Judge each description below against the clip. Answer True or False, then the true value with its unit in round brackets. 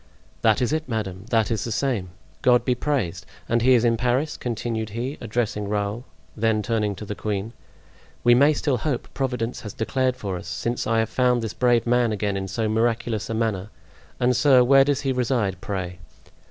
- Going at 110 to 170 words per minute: False (195 wpm)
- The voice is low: True (115 Hz)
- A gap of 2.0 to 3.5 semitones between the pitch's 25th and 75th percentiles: True (2.9 semitones)